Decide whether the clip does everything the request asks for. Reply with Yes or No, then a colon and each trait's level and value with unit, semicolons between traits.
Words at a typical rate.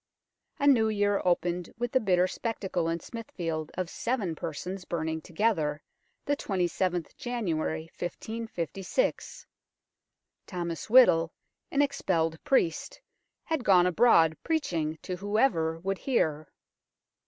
No: slow, 110 wpm